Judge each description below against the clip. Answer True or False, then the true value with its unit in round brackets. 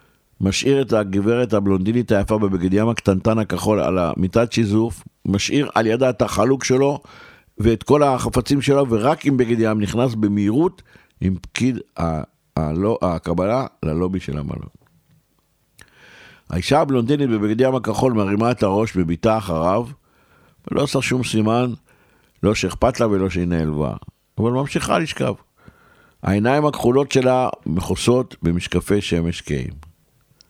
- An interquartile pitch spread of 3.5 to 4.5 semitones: False (5.1 semitones)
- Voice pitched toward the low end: True (110 Hz)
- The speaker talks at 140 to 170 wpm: False (120 wpm)